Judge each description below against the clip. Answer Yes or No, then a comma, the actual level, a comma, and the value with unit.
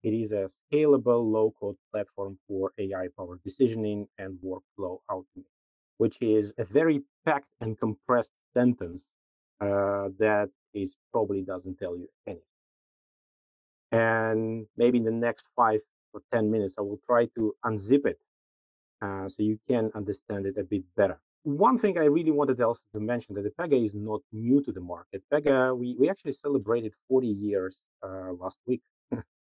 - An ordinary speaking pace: Yes, average, 160 wpm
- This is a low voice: Yes, low, 110 Hz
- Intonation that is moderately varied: Yes, average, 3.8 semitones